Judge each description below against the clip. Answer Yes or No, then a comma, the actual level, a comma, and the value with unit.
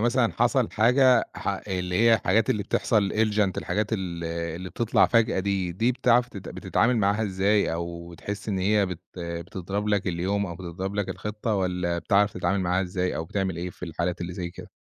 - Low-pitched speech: Yes, very low, 95 Hz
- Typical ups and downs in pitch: Yes, average, 3.2 semitones